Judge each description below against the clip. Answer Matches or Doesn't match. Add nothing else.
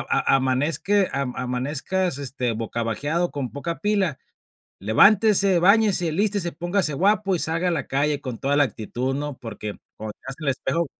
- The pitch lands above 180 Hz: Doesn't match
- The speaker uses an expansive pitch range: Matches